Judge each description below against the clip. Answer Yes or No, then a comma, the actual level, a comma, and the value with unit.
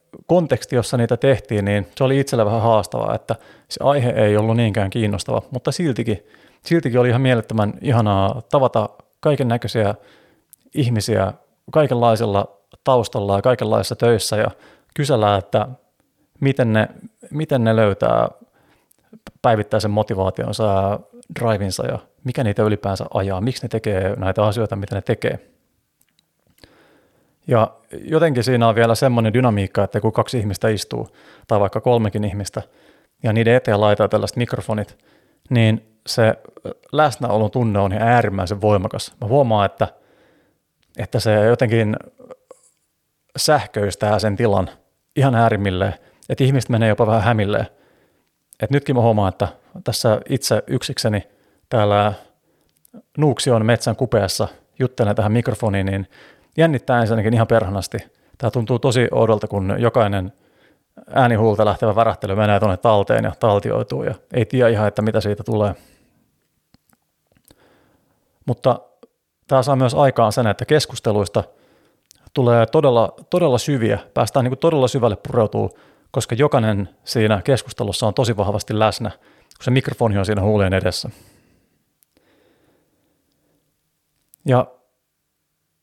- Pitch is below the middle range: Yes, low, 115 Hz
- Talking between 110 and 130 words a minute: Yes, average, 125 wpm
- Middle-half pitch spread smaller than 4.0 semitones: Yes, average, 3.6 semitones